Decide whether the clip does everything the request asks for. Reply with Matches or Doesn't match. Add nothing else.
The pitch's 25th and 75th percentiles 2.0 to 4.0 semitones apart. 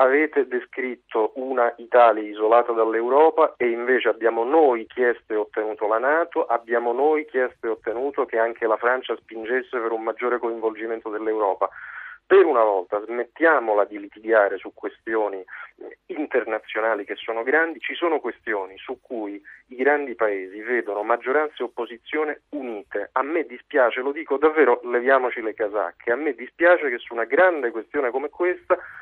Doesn't match